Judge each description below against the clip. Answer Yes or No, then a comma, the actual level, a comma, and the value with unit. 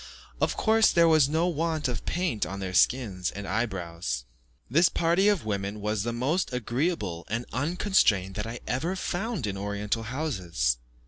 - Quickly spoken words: No, average, 170 wpm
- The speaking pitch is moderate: No, low, 120 Hz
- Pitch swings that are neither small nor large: No, wide, 8.9 semitones